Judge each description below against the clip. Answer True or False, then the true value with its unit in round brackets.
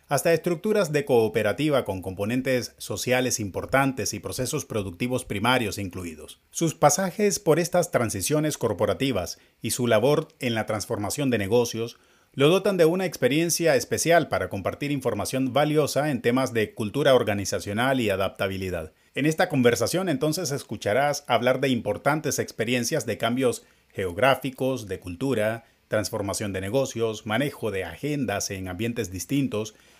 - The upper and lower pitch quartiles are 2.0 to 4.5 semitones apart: False (5.2 semitones)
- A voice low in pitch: True (125 Hz)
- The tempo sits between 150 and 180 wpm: False (135 wpm)